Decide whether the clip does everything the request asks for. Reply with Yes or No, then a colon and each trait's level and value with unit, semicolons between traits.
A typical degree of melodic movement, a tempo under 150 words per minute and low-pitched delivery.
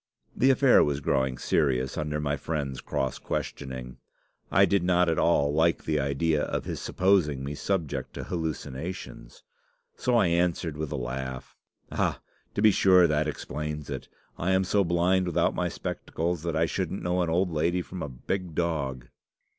No: average, 4.1 semitones; average, 170 wpm; very low, 80 Hz